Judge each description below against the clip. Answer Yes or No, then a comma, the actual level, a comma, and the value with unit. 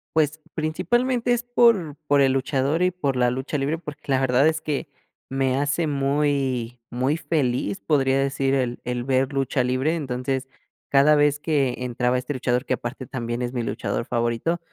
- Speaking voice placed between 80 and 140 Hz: Yes, low, 135 Hz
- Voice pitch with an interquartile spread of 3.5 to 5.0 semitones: No, average, 3.0 semitones